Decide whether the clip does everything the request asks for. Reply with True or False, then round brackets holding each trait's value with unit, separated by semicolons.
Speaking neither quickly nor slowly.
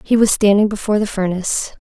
True (195 wpm)